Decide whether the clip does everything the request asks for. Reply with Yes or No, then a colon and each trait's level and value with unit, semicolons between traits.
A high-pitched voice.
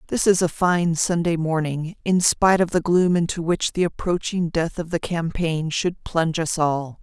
No: medium, 170 Hz